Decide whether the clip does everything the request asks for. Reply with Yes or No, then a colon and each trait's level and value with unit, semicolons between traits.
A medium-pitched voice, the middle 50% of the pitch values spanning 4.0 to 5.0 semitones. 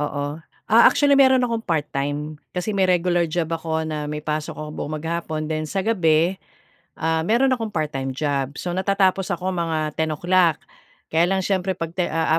No: medium, 165 Hz; average, 3.5 semitones